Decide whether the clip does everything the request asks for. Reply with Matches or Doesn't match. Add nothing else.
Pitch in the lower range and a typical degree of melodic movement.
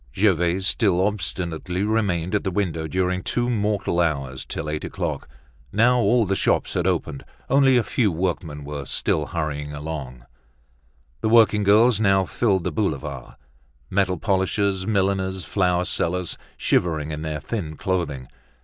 Matches